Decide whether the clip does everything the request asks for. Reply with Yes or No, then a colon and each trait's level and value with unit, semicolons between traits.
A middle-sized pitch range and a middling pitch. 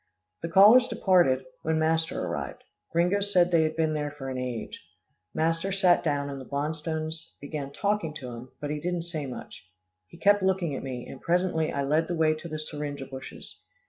Yes: average, 3.6 semitones; medium, 160 Hz